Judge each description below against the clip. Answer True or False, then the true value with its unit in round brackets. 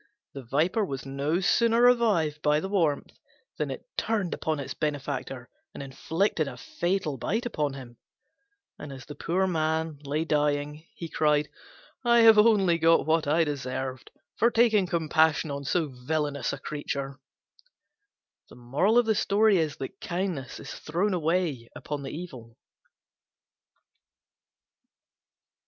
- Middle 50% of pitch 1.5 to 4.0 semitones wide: False (4.8 semitones)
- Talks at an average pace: False (125 wpm)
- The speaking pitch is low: False (155 Hz)